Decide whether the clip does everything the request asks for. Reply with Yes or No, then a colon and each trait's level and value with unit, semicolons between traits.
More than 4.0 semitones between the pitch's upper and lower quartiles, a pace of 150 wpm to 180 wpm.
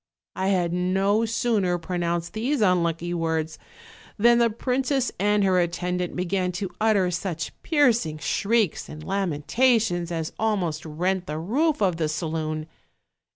No: average, 4.4 semitones; slow, 135 wpm